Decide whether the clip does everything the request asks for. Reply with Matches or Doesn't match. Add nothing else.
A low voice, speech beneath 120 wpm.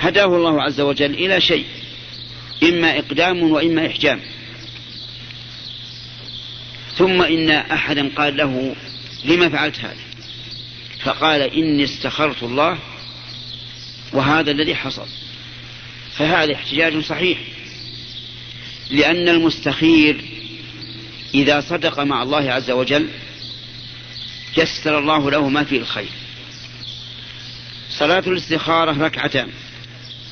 Matches